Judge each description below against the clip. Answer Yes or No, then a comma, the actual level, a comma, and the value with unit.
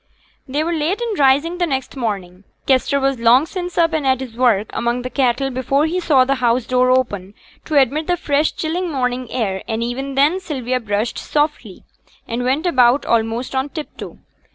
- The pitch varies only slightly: No, average, 4.0 semitones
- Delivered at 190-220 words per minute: Yes, average, 195 wpm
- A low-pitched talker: No, very high, 265 Hz